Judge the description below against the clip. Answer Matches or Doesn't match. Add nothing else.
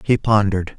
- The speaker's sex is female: Doesn't match